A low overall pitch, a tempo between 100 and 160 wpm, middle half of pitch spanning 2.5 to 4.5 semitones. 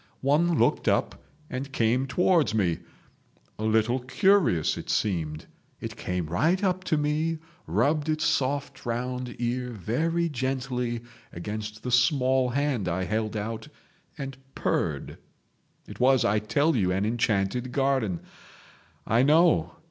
No: low, 125 Hz; slow, 135 wpm; average, 5.1 semitones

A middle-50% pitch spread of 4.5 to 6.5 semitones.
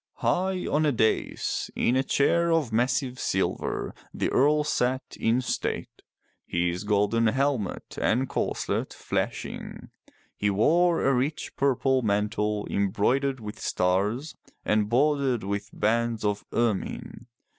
Yes: average, 4.8 semitones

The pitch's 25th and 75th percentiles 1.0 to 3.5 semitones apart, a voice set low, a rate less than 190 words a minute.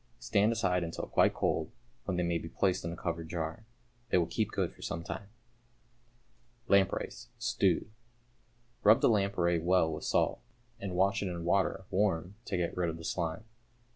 Yes: average, 2.9 semitones; very low, 90 Hz; average, 175 wpm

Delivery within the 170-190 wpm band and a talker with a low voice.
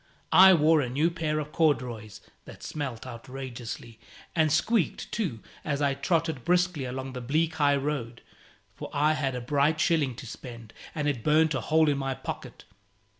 No: average, 175 wpm; medium, 145 Hz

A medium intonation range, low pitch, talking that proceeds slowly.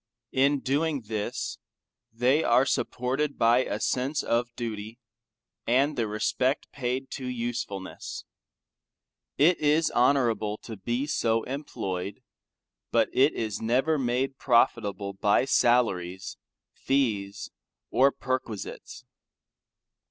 Yes: average, 3.7 semitones; low, 120 Hz; slow, 105 wpm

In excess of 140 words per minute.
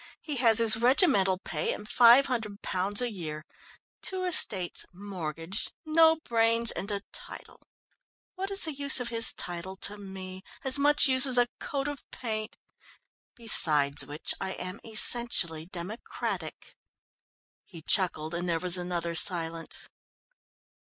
No: slow, 135 wpm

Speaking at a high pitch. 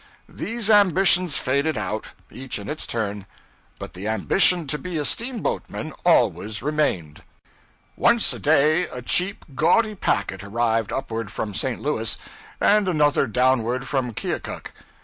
No: low, 135 Hz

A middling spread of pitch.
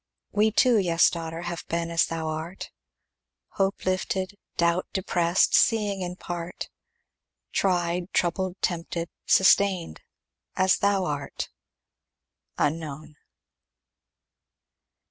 No: narrow, 2.2 semitones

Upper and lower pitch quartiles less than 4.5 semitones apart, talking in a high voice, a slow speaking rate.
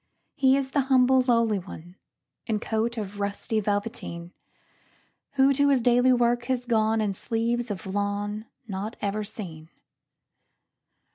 Yes: average, 3.4 semitones; high, 225 Hz; slow, 120 wpm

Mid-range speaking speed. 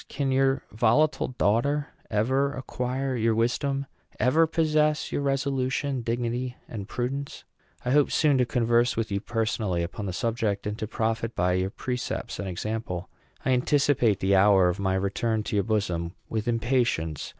Yes: average, 160 wpm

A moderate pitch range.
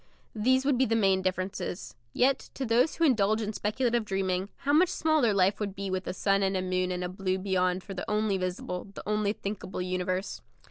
Yes: average, 3.5 semitones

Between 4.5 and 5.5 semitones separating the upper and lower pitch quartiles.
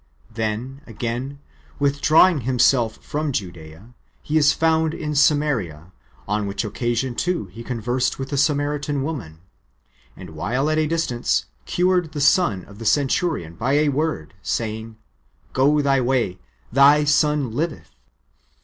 Yes: average, 5.0 semitones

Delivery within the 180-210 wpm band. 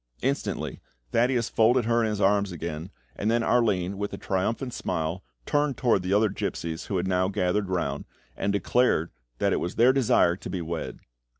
Yes: average, 185 wpm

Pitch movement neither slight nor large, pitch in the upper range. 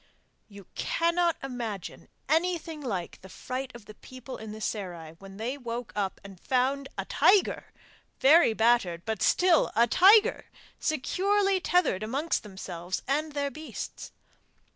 No: wide, 7.3 semitones; very high, 250 Hz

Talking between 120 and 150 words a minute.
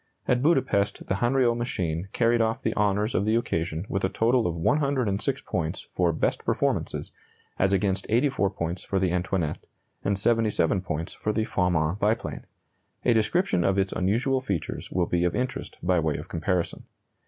No: average, 170 wpm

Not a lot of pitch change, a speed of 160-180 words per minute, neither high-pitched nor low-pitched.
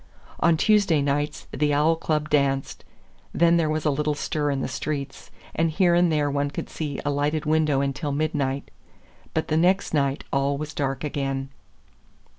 Yes: narrow, 2.0 semitones; average, 175 wpm; medium, 150 Hz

